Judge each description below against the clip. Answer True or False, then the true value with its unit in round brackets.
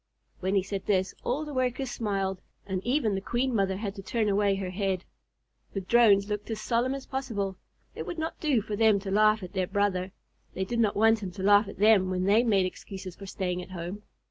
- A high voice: True (205 Hz)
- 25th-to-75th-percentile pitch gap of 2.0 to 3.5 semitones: True (2.9 semitones)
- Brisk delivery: True (225 wpm)